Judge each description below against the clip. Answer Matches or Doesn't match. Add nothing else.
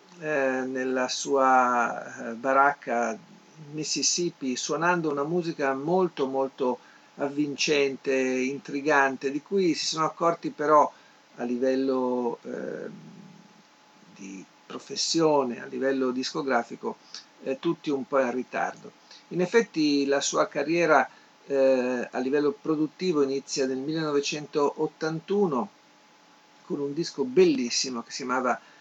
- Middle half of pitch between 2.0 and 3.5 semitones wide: Matches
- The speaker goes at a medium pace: Doesn't match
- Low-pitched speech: Doesn't match